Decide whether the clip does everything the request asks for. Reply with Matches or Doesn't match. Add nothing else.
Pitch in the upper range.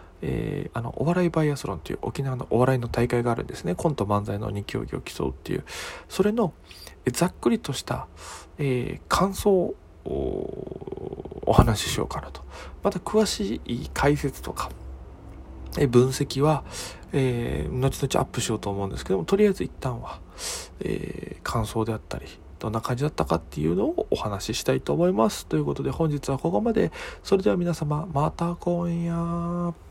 Doesn't match